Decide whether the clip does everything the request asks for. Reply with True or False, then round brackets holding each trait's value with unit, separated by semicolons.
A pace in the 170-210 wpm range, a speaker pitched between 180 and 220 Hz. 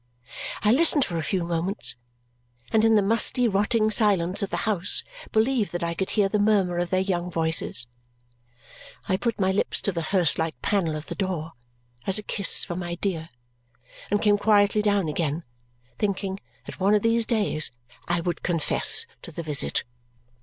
True (180 wpm; 190 Hz)